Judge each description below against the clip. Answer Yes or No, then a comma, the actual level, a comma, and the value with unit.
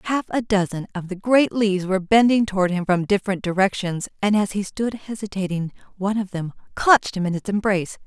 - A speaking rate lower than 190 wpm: No, average, 200 wpm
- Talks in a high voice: Yes, high, 200 Hz